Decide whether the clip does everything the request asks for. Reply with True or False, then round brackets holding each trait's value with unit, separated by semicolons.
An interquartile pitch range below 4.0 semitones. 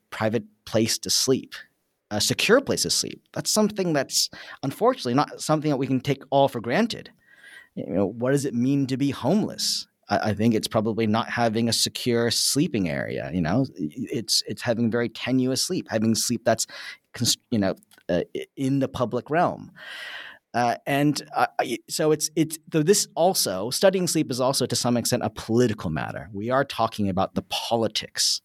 False (5.1 semitones)